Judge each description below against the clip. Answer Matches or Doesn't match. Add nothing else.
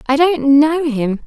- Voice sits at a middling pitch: Doesn't match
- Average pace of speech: Matches